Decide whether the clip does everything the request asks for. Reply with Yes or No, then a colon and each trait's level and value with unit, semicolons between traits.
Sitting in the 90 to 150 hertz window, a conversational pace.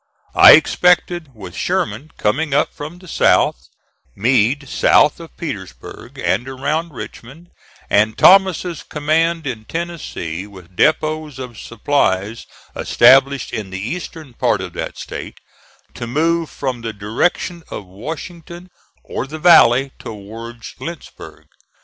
No: low, 135 Hz; slow, 125 wpm